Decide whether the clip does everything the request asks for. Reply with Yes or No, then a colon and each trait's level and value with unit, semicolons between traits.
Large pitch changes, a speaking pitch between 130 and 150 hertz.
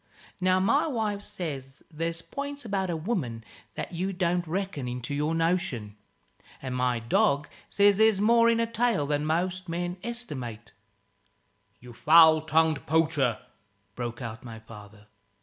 No: wide, 7.4 semitones; medium, 165 Hz